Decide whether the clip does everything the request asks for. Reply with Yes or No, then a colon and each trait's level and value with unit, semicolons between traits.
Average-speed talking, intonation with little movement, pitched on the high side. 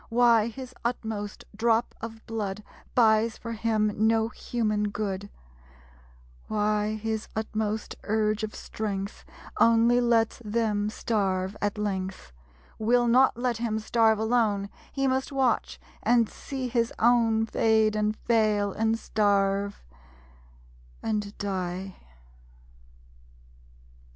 No: slow, 110 wpm; narrow, 1.8 semitones; high, 220 Hz